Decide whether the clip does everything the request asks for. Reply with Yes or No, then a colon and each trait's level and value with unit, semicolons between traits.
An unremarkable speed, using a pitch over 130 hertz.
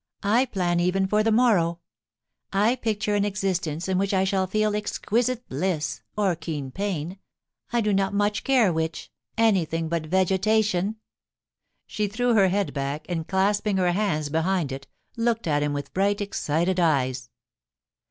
Yes: average, 160 wpm; high, 190 Hz